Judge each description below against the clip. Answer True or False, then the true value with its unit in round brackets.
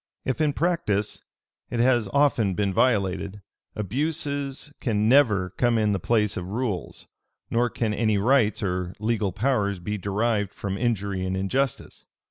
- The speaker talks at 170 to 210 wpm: False (145 wpm)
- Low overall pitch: True (105 Hz)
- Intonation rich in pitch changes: False (4.2 semitones)